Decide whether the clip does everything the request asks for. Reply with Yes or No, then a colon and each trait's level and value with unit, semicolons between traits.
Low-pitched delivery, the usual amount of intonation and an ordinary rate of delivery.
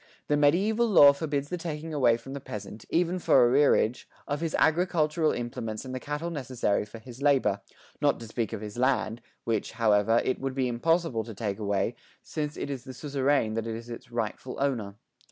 Yes: low, 130 Hz; average, 4.5 semitones; average, 190 wpm